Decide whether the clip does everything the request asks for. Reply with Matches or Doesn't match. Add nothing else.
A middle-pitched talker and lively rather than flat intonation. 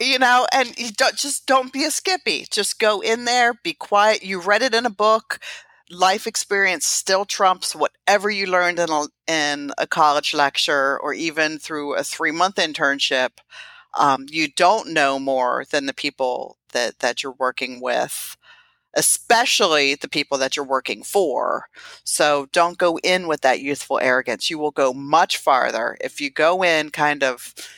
Matches